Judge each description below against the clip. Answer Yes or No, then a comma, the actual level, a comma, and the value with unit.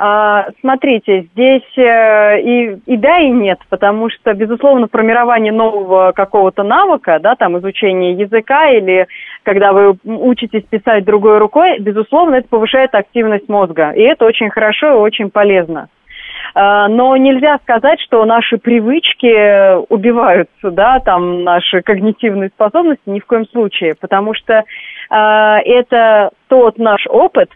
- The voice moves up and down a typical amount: Yes, average, 3.1 semitones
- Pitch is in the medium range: No, high, 220 Hz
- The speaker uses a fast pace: No, average, 130 wpm